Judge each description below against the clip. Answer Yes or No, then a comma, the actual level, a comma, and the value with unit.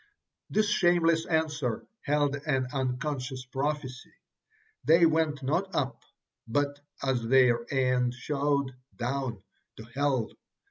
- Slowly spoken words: Yes, slow, 105 wpm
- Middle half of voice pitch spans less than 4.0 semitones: Yes, average, 2.9 semitones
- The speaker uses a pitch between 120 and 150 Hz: Yes, medium, 140 Hz